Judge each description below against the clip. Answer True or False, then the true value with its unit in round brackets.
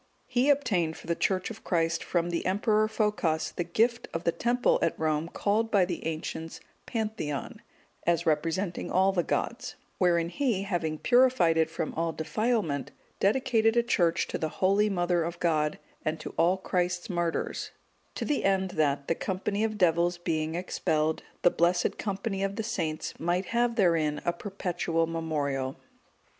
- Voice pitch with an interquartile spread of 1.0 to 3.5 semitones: False (4.1 semitones)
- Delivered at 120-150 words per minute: False (165 wpm)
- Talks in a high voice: False (175 Hz)